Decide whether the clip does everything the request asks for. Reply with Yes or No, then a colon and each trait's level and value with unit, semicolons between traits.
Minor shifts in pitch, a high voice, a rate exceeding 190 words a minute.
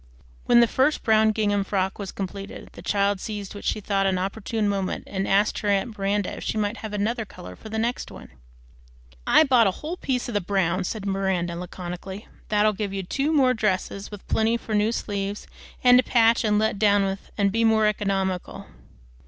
Yes: narrow, 2.2 semitones; high, 205 Hz; average, 200 wpm